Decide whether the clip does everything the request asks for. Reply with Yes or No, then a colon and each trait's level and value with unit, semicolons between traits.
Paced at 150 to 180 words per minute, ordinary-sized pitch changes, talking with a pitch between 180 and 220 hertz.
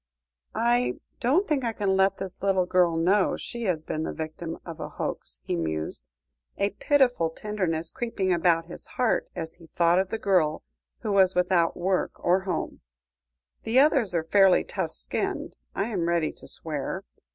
Yes: average, 175 wpm; average, 4.2 semitones; medium, 185 Hz